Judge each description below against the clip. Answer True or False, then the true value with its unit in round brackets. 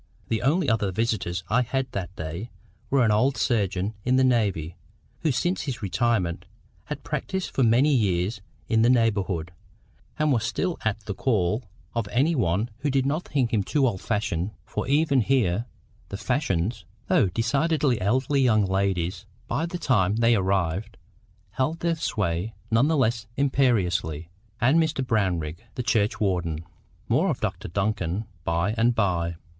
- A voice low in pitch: True (110 Hz)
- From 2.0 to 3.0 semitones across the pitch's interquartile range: False (5.5 semitones)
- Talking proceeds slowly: False (155 wpm)